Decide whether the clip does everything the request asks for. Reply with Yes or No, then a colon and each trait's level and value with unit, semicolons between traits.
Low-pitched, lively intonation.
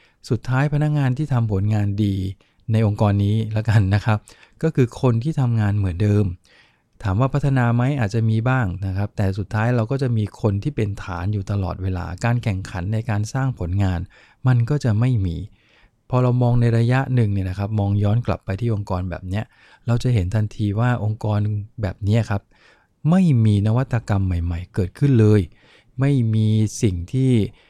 No: low, 110 Hz; average, 3.4 semitones